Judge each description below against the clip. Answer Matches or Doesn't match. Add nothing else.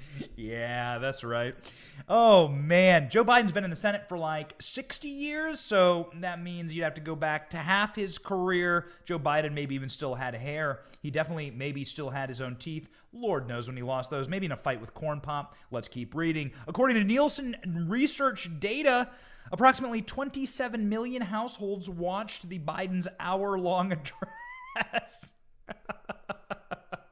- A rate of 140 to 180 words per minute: Matches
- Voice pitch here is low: Doesn't match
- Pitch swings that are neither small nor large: Doesn't match